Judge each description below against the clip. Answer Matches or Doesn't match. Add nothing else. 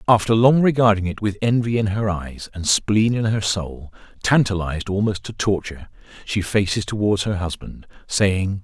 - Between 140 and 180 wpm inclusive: Matches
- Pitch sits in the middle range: Doesn't match